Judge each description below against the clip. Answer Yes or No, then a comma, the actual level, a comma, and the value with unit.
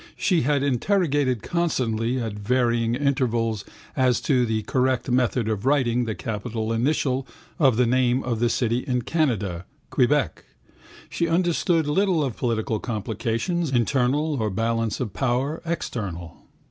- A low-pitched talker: Yes, low, 125 Hz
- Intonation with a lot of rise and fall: No, average, 3.8 semitones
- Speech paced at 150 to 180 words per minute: No, slow, 135 wpm